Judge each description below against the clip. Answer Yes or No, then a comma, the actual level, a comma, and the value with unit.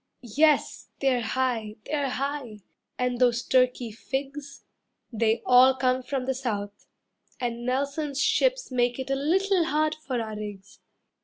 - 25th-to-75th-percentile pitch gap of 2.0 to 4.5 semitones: Yes, average, 2.9 semitones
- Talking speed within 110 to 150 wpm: Yes, average, 140 wpm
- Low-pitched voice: No, very high, 255 Hz